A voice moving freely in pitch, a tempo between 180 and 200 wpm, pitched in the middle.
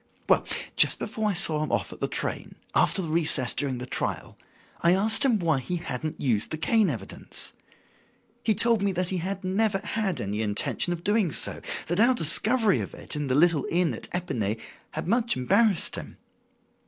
Yes: wide, 6.0 semitones; average, 190 wpm; medium, 175 Hz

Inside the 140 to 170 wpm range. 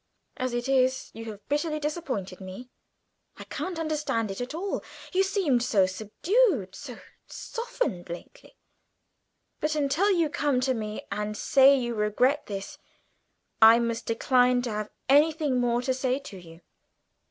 Yes: average, 150 wpm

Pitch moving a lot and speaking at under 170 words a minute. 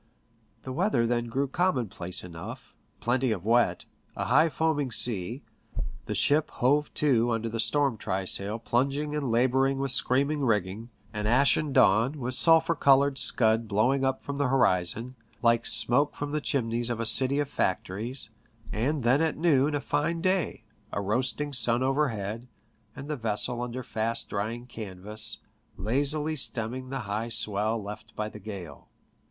No: average, 4.2 semitones; average, 155 wpm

